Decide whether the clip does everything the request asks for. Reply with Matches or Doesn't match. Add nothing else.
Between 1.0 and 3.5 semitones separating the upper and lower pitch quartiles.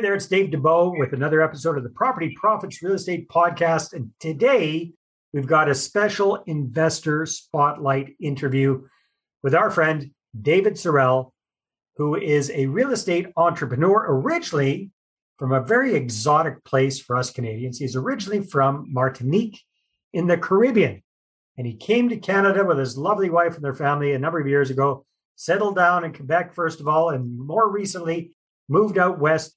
Doesn't match